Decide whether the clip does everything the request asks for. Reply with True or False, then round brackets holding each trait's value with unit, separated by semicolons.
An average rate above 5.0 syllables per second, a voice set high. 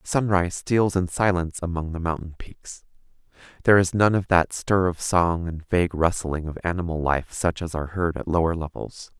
False (5.3 syllables/s; 85 Hz)